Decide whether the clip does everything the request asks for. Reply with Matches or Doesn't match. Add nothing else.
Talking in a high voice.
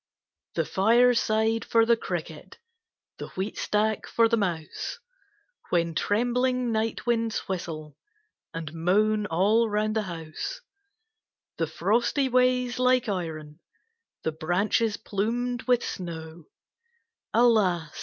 Matches